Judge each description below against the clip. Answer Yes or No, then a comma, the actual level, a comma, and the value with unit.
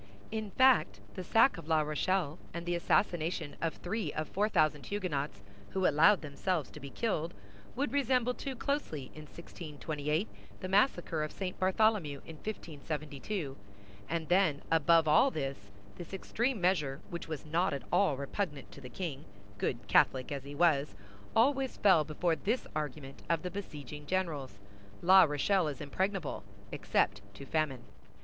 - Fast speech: No, average, 155 wpm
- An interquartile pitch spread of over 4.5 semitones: Yes, average, 4.9 semitones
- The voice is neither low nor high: Yes, medium, 160 Hz